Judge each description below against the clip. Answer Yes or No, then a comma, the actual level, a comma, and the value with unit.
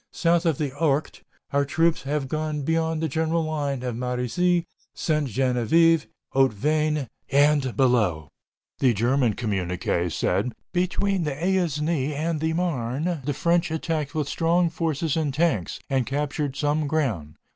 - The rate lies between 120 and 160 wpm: Yes, average, 140 wpm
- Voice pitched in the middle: Yes, medium, 150 Hz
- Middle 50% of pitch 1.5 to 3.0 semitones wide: No, average, 3.8 semitones